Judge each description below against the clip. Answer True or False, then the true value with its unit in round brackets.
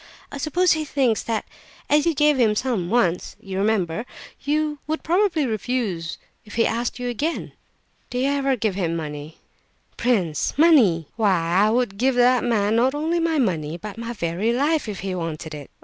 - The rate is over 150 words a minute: True (180 wpm)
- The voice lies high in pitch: True (230 Hz)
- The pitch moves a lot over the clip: True (7.0 semitones)